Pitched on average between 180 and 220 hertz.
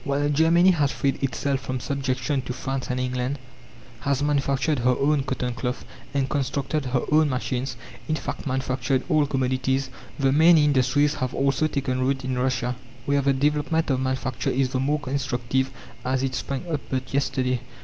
No: low, 135 Hz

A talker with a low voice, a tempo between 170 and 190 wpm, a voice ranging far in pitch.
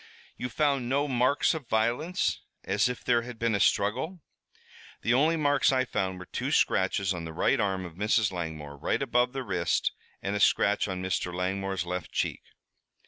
Yes: low, 105 Hz; average, 185 wpm; wide, 5.7 semitones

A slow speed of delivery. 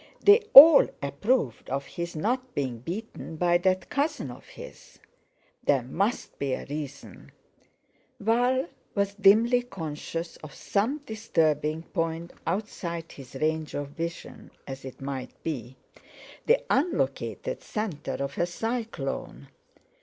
Yes: slow, 125 wpm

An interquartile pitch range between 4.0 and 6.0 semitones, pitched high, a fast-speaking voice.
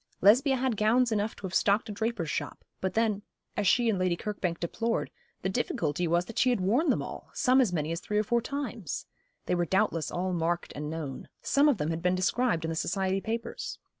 Yes: average, 5.0 semitones; high, 200 Hz; fast, 225 wpm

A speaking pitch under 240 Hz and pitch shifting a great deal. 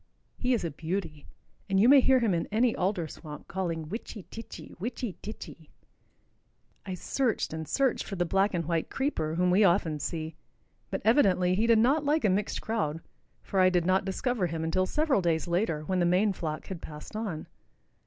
No: medium, 185 Hz; average, 5.0 semitones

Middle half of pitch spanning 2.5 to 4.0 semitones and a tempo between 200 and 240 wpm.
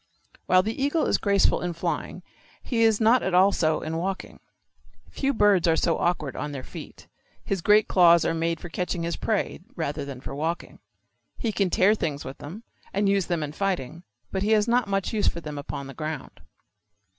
No: average, 4.5 semitones; fast, 205 wpm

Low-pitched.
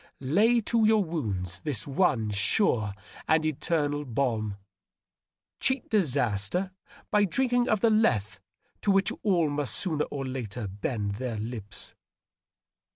No: medium, 145 Hz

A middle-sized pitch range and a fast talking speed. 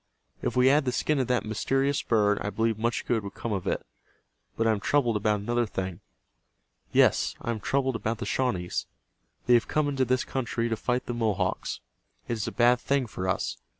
Yes: average, 3.2 semitones; fast, 210 wpm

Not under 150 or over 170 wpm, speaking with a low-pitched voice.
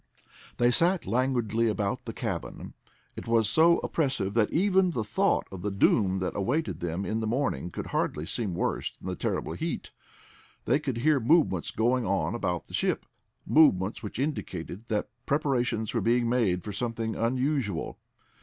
Yes: average, 165 wpm; low, 115 Hz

